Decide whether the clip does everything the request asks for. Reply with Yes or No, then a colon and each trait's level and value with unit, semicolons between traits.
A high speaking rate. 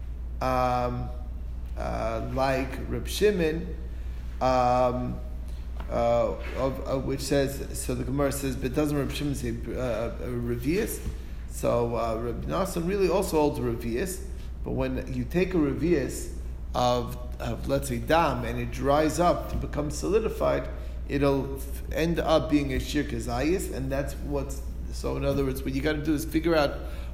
No: average, 155 wpm